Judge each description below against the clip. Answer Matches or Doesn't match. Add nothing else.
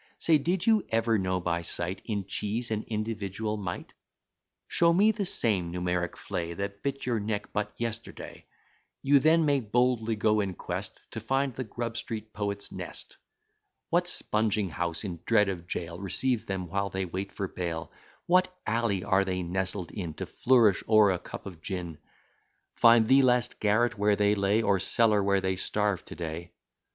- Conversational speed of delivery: Matches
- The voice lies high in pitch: Doesn't match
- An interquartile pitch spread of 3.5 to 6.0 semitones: Matches